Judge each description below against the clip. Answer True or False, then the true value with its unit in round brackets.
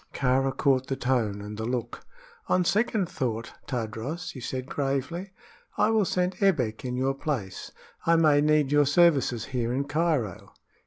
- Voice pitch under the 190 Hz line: True (135 Hz)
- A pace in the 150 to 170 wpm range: True (160 wpm)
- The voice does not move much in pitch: False (5.1 semitones)